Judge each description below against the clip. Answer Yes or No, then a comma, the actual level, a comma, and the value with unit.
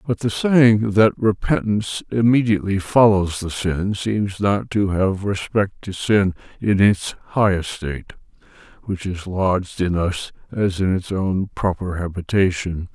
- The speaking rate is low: No, average, 145 wpm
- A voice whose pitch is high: No, low, 100 Hz